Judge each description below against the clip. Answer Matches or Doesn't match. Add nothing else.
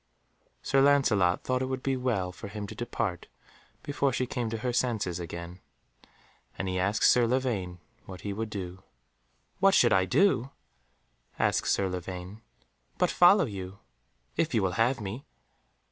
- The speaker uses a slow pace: Doesn't match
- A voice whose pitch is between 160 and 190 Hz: Doesn't match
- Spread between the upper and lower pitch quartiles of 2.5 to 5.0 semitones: Doesn't match